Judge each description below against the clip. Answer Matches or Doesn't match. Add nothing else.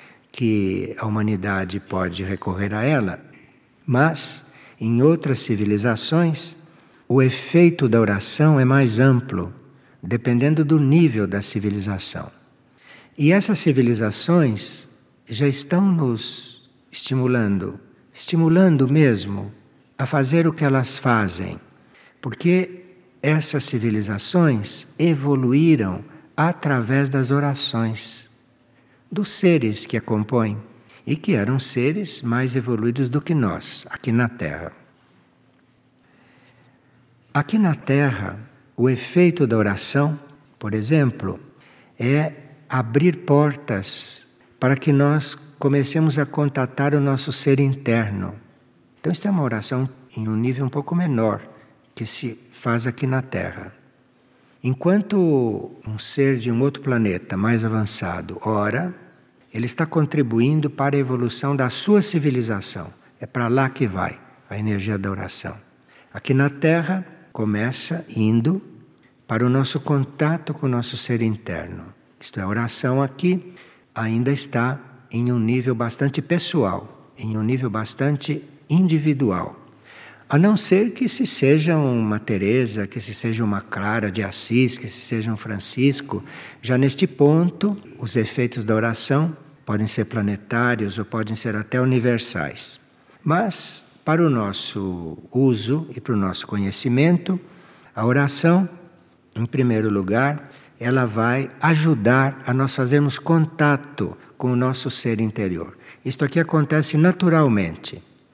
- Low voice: Matches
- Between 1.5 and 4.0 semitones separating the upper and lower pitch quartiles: Doesn't match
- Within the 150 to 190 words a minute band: Doesn't match